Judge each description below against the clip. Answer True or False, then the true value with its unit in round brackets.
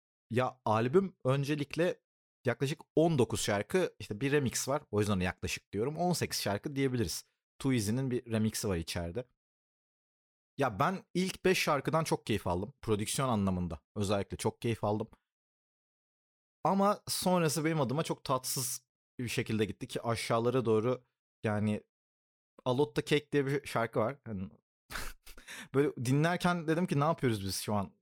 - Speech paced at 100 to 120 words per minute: False (140 wpm)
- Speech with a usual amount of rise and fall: False (5.9 semitones)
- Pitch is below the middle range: True (125 Hz)